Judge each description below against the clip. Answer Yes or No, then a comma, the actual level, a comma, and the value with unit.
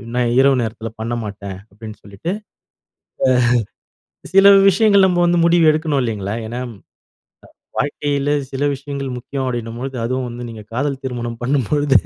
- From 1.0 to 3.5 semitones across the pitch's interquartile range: No, average, 4.0 semitones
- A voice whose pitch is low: Yes, low, 130 Hz